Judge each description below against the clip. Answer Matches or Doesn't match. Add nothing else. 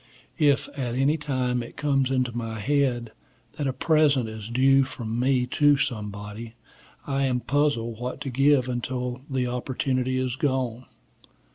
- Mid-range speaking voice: Doesn't match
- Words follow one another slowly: Doesn't match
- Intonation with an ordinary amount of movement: Doesn't match